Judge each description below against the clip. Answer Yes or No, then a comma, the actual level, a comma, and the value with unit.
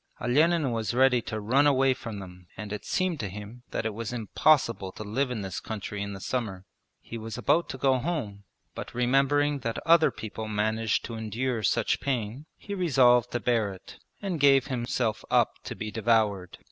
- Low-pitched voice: Yes, low, 115 Hz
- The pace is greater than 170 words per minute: Yes, average, 190 wpm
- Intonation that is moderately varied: Yes, average, 4.2 semitones